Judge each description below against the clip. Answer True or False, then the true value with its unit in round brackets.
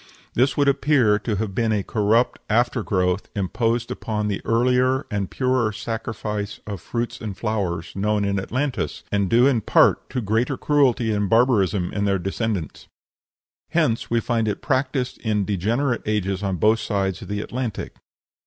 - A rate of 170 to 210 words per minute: False (160 wpm)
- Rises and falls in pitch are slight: False (3.3 semitones)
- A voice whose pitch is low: True (110 Hz)